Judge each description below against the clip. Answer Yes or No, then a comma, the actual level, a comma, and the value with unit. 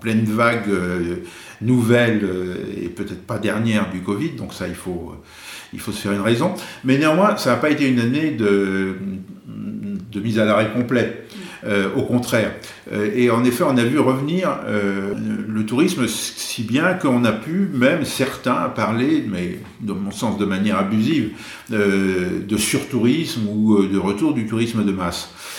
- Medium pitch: No, low, 110 Hz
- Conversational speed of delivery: Yes, average, 175 wpm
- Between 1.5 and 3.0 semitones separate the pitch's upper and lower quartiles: No, average, 3.8 semitones